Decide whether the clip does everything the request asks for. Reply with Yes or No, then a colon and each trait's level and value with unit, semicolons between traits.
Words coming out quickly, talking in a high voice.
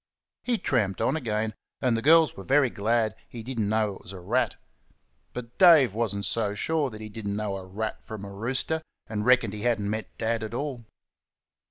No: fast, 220 wpm; low, 110 Hz